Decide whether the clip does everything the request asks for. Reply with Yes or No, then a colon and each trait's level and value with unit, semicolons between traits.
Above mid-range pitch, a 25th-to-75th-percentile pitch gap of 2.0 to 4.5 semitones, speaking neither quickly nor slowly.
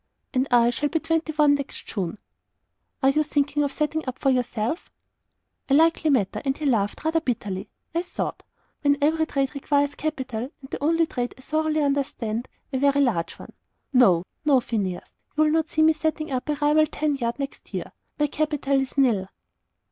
Yes: very high, 280 Hz; average, 3.7 semitones; average, 185 wpm